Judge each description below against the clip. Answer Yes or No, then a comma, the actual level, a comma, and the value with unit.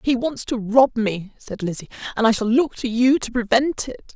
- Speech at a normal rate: No, fast, 230 wpm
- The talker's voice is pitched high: Yes, high, 235 Hz